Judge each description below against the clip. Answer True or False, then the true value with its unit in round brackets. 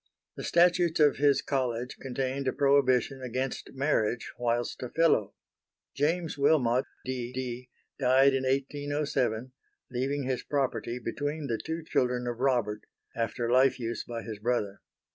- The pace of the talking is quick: False (140 wpm)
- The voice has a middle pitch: False (130 Hz)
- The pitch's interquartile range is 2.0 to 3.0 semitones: True (2.7 semitones)